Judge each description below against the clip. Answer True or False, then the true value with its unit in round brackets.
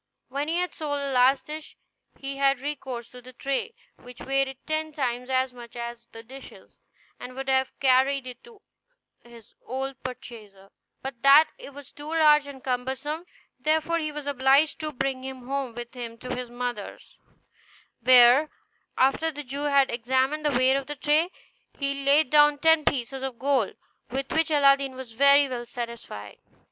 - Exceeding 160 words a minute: True (175 wpm)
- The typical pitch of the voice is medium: False (270 Hz)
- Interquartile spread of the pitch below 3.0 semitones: True (2.6 semitones)